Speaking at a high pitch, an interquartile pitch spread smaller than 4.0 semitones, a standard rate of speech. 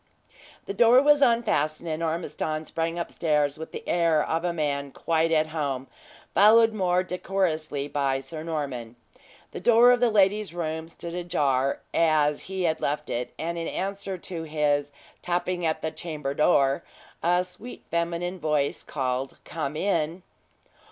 No: medium, 165 Hz; average, 3.4 semitones; average, 150 wpm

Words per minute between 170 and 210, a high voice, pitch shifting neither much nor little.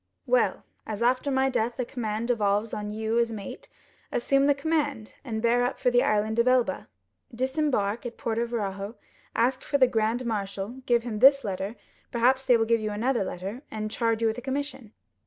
Yes: average, 190 wpm; high, 235 Hz; average, 3.1 semitones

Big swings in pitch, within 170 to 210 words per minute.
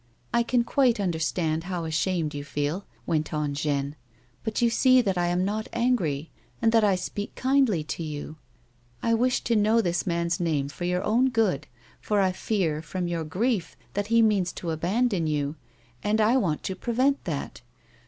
Yes: wide, 6.2 semitones; average, 190 wpm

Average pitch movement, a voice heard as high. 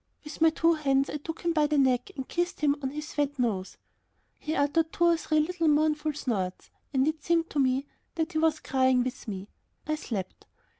Yes: average, 3.3 semitones; very high, 295 Hz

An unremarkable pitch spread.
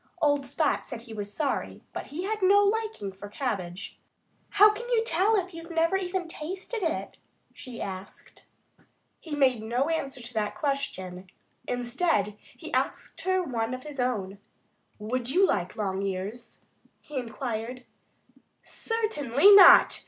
No: wide, 8.5 semitones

